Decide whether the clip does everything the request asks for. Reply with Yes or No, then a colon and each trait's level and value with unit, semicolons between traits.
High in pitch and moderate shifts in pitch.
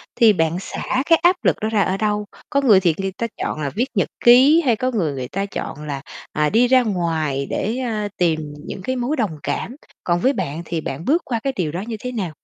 No: high, 205 Hz; wide, 7.1 semitones